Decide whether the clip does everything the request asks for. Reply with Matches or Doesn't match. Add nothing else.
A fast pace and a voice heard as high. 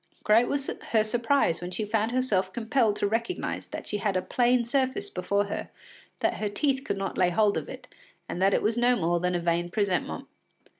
Matches